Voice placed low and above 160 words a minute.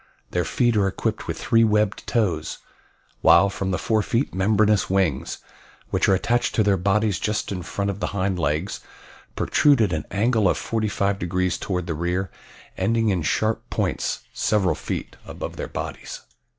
Yes: low, 100 Hz; average, 170 wpm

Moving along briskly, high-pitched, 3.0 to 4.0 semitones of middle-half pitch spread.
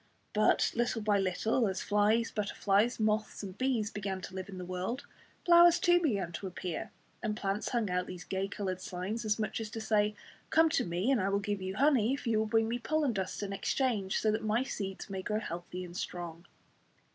Yes: fast, 215 wpm; high, 210 Hz; average, 3.3 semitones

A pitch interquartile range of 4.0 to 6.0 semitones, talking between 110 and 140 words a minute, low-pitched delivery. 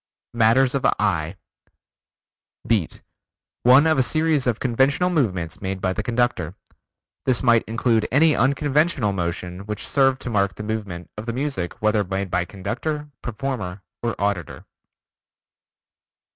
Yes: wide, 5.4 semitones; slow, 135 wpm; low, 115 Hz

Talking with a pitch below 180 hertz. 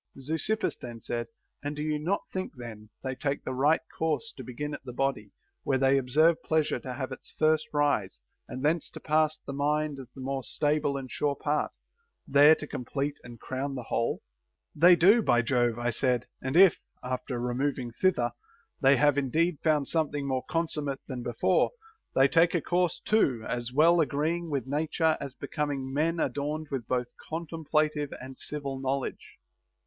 Yes: medium, 140 Hz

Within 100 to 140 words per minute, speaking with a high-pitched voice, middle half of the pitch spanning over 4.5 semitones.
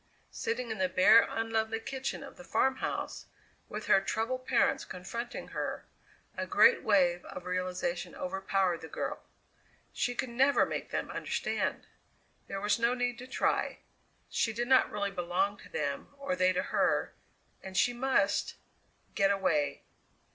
No: average, 150 wpm; high, 210 Hz; average, 5.0 semitones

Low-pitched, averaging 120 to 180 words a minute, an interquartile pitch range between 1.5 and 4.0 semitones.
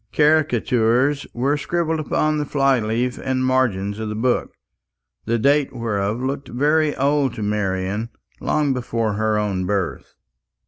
No: low, 125 Hz; average, 140 wpm; average, 5.0 semitones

